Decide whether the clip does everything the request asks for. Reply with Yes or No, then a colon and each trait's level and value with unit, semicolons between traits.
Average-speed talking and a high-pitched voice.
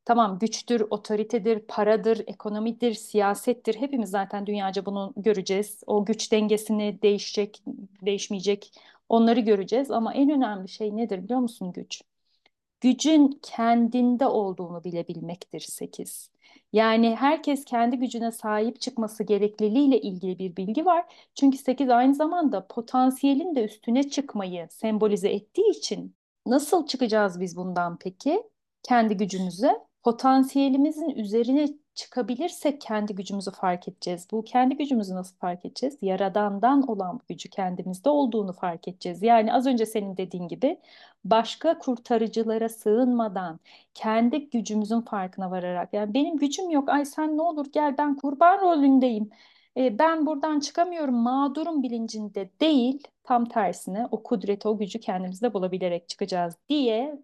Yes: average, 130 wpm; high, 230 Hz